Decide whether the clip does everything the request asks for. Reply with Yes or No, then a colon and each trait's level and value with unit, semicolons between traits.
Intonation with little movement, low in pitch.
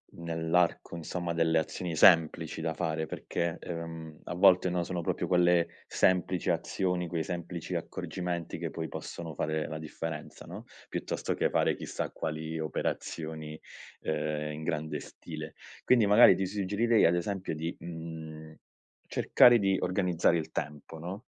Yes: narrow, 2.1 semitones; very low, 85 Hz